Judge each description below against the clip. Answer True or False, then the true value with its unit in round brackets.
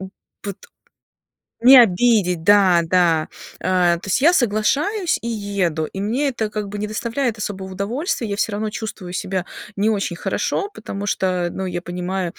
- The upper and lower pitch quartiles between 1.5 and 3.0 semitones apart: False (3.6 semitones)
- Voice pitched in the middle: False (200 Hz)